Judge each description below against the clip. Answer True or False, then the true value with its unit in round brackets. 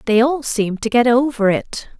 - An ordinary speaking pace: False (210 wpm)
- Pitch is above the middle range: True (240 Hz)